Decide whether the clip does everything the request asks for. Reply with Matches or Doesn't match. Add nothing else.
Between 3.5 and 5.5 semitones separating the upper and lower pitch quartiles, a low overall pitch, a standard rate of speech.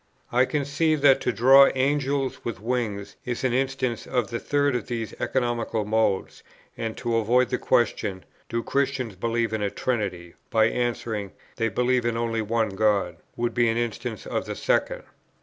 Doesn't match